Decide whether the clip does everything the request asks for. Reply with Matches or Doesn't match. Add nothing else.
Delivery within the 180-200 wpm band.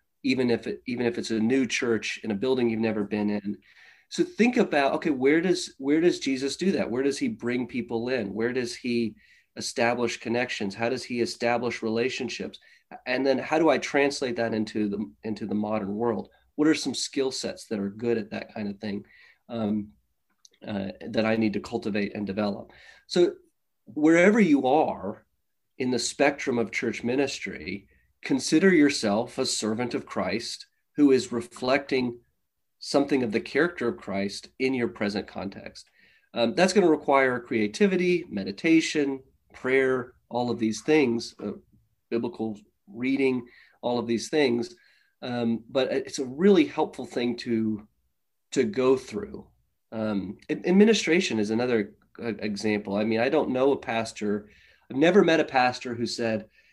Doesn't match